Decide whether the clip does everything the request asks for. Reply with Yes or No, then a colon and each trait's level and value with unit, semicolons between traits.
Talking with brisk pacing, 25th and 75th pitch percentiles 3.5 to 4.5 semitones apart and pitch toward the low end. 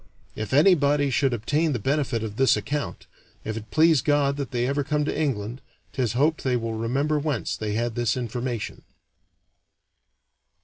No: average, 165 wpm; average, 4.1 semitones; low, 130 Hz